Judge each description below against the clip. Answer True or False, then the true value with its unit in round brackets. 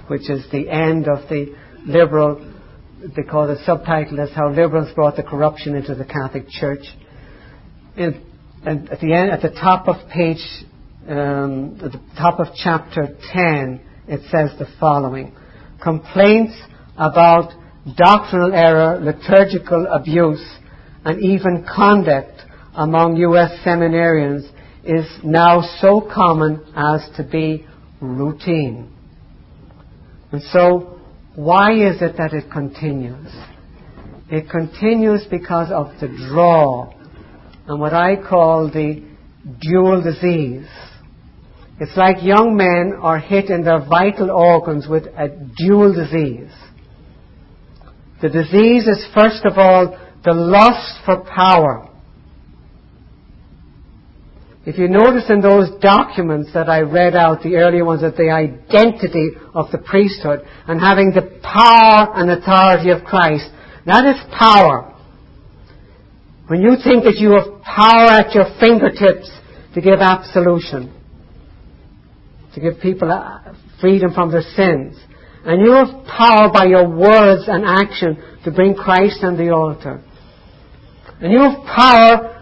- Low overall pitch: False (170 Hz)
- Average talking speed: False (125 wpm)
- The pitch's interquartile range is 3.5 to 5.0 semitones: True (4.0 semitones)